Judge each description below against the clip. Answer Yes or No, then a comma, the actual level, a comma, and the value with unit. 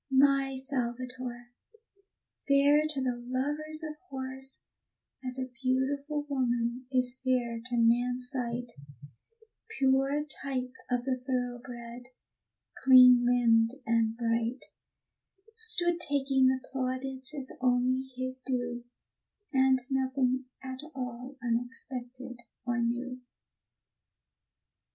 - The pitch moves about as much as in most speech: No, narrow, 1.6 semitones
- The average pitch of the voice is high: Yes, very high, 255 Hz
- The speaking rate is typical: No, slow, 100 wpm